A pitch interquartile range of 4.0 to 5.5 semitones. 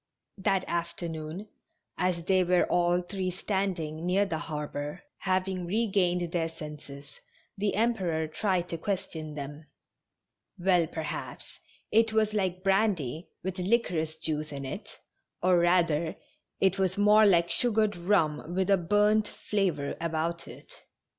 No: average, 3.5 semitones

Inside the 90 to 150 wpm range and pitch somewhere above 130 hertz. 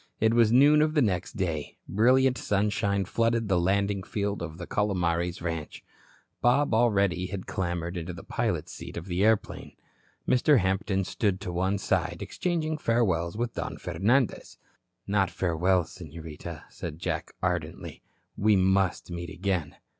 No: average, 145 wpm; very low, 95 Hz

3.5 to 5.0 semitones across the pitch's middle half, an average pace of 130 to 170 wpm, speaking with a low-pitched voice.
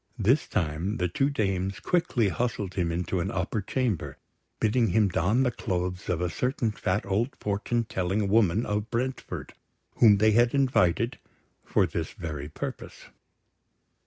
Yes: average, 4.5 semitones; average, 150 wpm; low, 105 Hz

